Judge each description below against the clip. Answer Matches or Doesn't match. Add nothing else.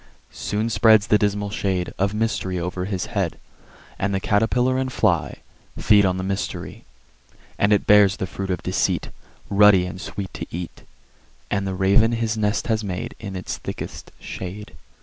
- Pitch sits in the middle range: Doesn't match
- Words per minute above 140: Matches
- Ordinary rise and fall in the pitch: Doesn't match